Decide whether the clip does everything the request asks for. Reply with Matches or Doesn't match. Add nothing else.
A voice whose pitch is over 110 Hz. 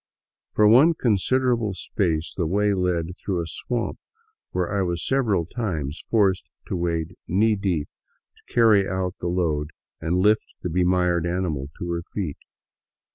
Doesn't match